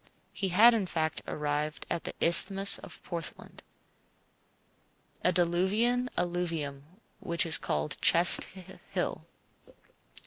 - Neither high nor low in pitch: Yes, medium, 175 Hz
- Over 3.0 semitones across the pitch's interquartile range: Yes, average, 3.4 semitones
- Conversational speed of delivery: No, slow, 105 wpm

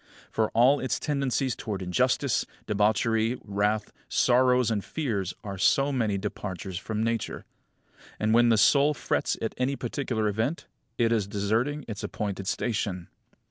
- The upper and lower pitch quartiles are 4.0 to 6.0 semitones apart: No, average, 3.6 semitones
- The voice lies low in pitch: Yes, low, 110 Hz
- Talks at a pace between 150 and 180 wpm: No, average, 140 wpm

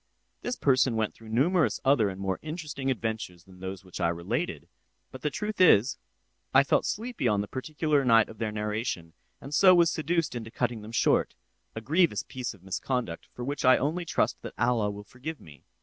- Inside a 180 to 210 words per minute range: Yes, average, 195 wpm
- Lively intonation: Yes, wide, 6.2 semitones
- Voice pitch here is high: No, low, 120 Hz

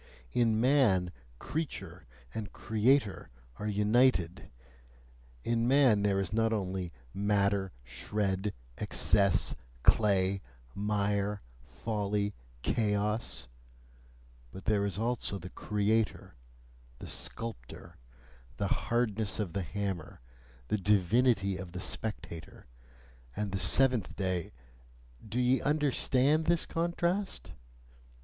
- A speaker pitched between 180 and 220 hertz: No, low, 105 Hz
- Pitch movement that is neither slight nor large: Yes, average, 3.3 semitones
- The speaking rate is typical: No, slow, 100 wpm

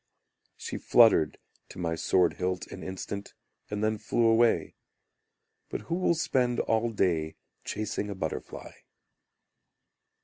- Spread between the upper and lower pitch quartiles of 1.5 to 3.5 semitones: No, average, 4.1 semitones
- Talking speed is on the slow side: Yes, slow, 125 wpm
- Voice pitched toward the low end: Yes, low, 105 Hz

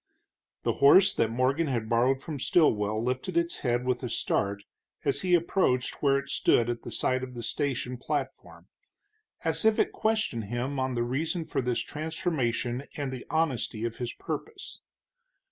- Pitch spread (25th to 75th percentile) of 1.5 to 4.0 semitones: No, average, 4.6 semitones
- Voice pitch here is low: Yes, low, 130 Hz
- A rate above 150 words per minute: Yes, average, 170 wpm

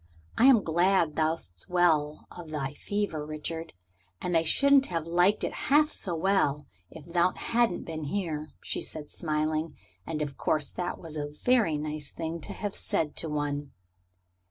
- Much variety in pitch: No, average, 3.0 semitones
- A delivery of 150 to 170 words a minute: Yes, average, 160 wpm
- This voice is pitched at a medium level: Yes, medium, 160 Hz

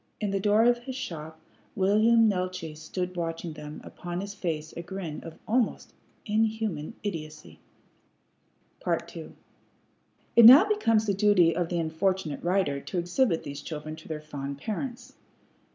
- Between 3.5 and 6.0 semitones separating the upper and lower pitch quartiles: Yes, average, 5.2 semitones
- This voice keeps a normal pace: Yes, average, 145 wpm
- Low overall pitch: No, medium, 180 Hz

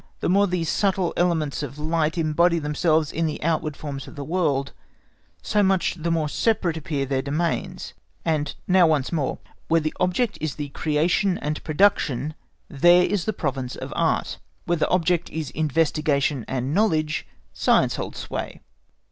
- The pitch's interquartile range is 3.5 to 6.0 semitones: No, average, 3.0 semitones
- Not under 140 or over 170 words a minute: Yes, average, 160 wpm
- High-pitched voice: No, medium, 160 Hz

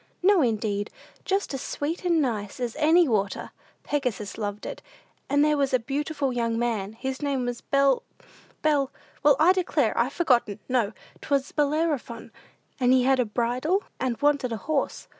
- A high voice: Yes, very high, 265 Hz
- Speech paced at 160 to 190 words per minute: Yes, average, 165 wpm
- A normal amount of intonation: Yes, average, 4.2 semitones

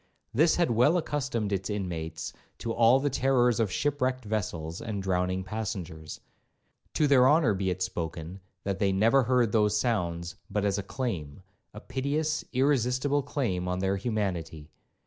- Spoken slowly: No, average, 150 wpm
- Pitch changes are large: Yes, wide, 5.7 semitones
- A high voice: No, low, 105 Hz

